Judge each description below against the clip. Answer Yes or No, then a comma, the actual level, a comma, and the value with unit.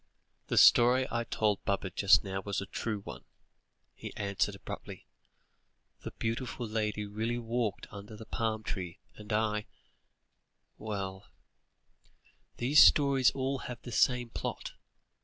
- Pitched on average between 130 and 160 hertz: No, low, 110 Hz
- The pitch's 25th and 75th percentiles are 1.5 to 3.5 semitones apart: Yes, average, 3.0 semitones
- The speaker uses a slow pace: Yes, slow, 130 wpm